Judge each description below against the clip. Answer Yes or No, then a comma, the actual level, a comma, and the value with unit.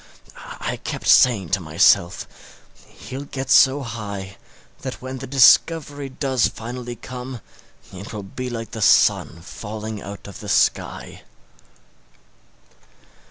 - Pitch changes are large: No, average, 4.3 semitones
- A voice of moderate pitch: No, low, 120 Hz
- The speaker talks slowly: Yes, slow, 115 wpm